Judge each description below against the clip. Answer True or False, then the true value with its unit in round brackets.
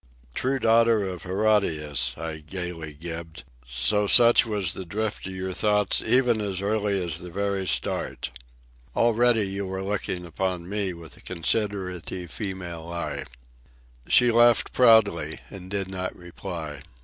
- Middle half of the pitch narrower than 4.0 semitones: True (3.6 semitones)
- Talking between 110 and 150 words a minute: True (140 wpm)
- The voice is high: False (95 Hz)